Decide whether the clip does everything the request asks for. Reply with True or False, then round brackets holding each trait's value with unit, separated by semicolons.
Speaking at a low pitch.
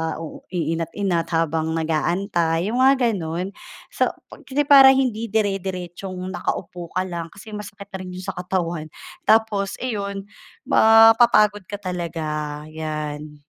False (185 Hz)